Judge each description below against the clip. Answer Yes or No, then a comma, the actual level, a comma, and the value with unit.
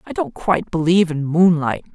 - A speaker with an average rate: Yes, average, 185 wpm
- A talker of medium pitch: Yes, medium, 175 Hz